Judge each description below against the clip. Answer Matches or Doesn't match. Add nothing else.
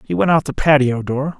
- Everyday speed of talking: Doesn't match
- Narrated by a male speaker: Matches